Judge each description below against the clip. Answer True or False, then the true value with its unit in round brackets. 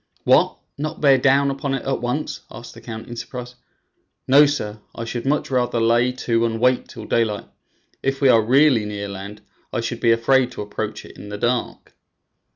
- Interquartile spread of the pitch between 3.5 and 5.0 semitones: False (3.0 semitones)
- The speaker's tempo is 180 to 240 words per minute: True (195 wpm)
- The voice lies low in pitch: True (120 Hz)